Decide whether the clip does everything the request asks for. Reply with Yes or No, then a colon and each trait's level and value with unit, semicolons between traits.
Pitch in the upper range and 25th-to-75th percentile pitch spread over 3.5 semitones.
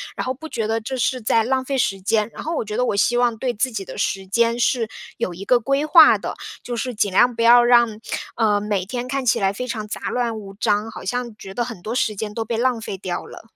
No: high, 230 Hz; average, 2.9 semitones